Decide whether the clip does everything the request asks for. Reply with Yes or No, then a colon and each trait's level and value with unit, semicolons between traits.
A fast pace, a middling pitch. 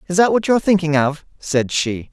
Yes: fast, 225 wpm; medium, 165 Hz